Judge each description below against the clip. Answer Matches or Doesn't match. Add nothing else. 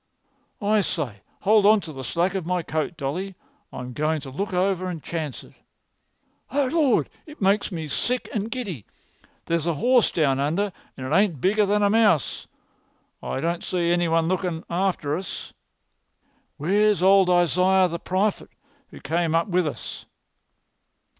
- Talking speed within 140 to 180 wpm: Matches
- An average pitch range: Matches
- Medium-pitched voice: Matches